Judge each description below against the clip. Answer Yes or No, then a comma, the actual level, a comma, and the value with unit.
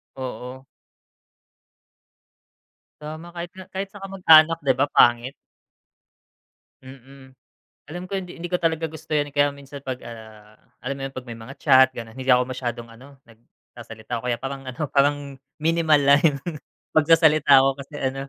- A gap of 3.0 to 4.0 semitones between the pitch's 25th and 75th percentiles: Yes, average, 3.6 semitones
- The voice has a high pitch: No, medium, 140 Hz